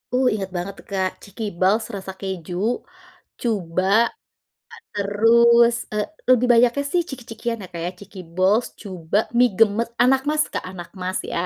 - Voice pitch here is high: Yes, high, 205 Hz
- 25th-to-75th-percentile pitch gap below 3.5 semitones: No, average, 4.0 semitones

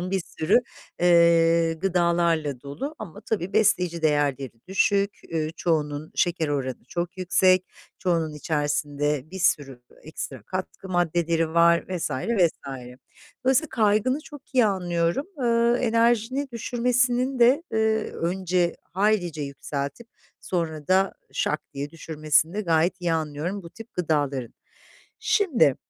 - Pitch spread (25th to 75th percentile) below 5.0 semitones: No, wide, 5.5 semitones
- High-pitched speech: No, medium, 175 Hz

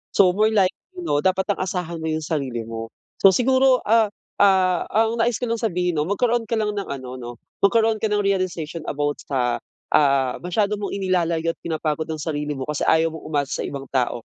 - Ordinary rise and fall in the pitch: No, wide, 5.9 semitones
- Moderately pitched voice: Yes, medium, 180 Hz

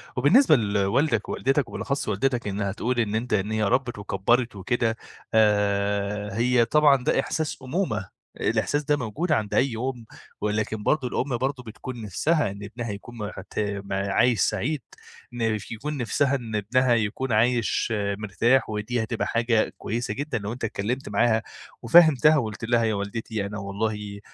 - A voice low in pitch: Yes, low, 115 Hz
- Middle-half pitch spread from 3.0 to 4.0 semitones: Yes, average, 3.6 semitones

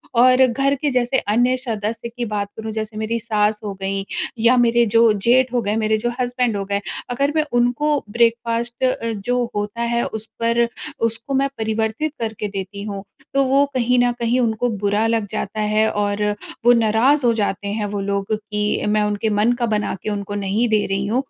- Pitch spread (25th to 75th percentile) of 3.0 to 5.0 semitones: No, narrow, 2.6 semitones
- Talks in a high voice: Yes, high, 225 Hz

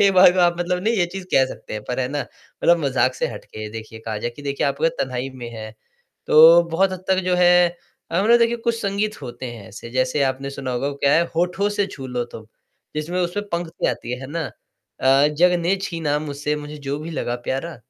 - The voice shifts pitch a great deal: Yes, wide, 5.7 semitones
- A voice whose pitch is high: No, medium, 150 Hz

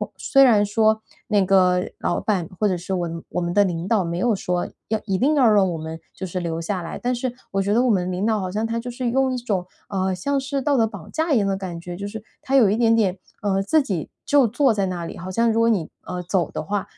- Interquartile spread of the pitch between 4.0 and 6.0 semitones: Yes, average, 4.3 semitones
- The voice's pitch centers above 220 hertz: No, high, 200 Hz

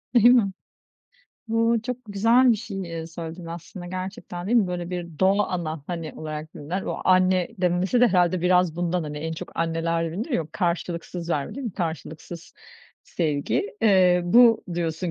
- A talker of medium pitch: Yes, medium, 180 Hz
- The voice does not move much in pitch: No, average, 3.0 semitones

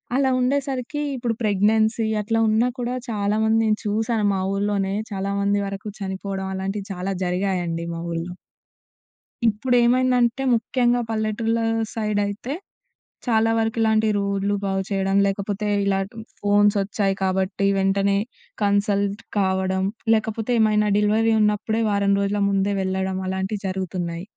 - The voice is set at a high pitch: Yes, high, 205 Hz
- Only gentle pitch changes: Yes, narrow, 2.3 semitones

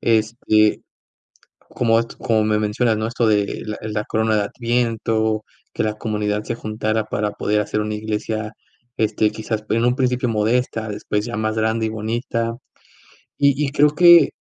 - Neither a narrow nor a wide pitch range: No, narrow, 1.4 semitones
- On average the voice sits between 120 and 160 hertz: No, low, 110 Hz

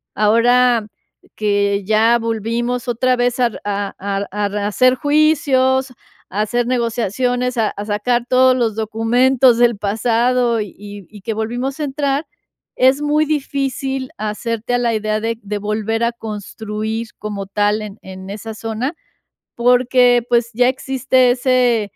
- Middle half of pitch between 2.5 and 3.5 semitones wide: Yes, average, 3.0 semitones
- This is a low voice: No, high, 235 Hz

